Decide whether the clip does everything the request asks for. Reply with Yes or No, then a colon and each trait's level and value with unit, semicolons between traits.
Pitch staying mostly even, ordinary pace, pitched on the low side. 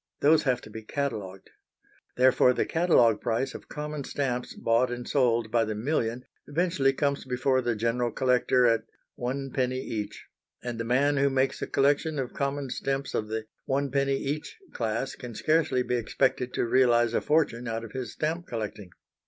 No: average, 3.1 semitones; average, 175 wpm; low, 125 Hz